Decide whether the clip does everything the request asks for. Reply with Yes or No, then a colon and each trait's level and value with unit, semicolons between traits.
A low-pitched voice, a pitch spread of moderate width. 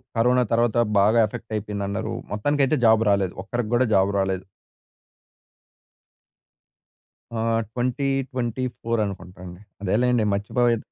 Yes: low, 115 Hz; average, 3.6 semitones